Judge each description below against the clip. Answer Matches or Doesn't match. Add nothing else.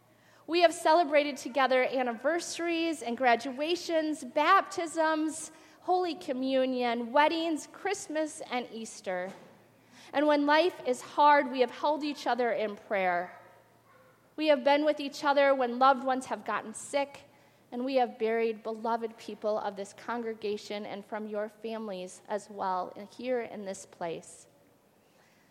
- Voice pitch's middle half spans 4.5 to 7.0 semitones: Matches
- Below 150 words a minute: Matches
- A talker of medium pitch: Doesn't match